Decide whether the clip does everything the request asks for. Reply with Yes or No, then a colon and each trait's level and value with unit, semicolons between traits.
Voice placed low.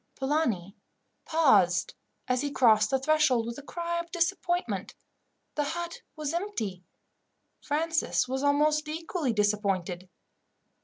No: very high, 285 Hz